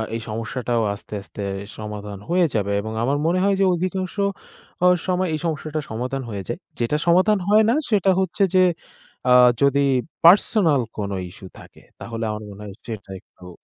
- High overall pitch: No, low, 135 Hz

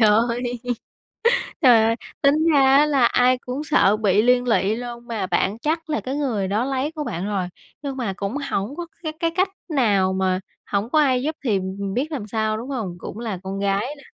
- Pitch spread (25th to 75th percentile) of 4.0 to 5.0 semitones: No, wide, 5.6 semitones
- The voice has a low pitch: No, high, 235 Hz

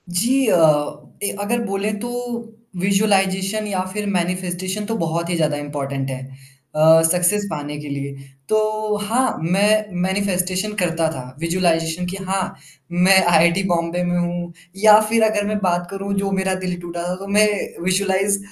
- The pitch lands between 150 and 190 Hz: Yes, medium, 185 Hz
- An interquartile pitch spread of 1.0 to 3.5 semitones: Yes, average, 3.0 semitones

